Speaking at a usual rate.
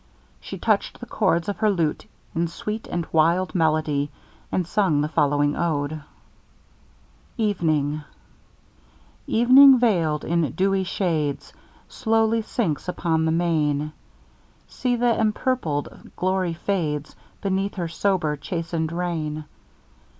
No: slow, 110 wpm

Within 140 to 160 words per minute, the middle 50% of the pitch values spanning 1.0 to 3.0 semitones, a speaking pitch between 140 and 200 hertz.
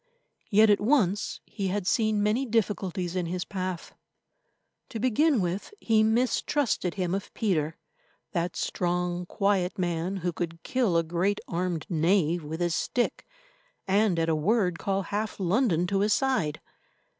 No: average, 150 wpm; average, 3.6 semitones; high, 190 Hz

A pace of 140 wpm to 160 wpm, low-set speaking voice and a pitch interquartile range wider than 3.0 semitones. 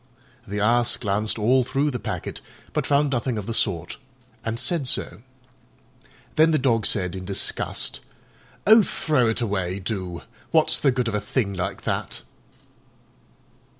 Yes: average, 150 wpm; low, 115 Hz; average, 4.7 semitones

